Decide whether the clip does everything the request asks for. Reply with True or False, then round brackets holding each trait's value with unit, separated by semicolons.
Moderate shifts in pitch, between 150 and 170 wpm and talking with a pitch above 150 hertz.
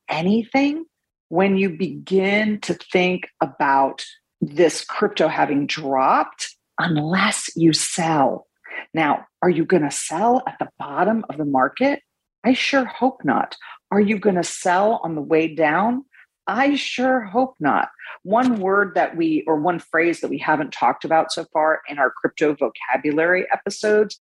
False (6.5 semitones; 155 wpm; 190 Hz)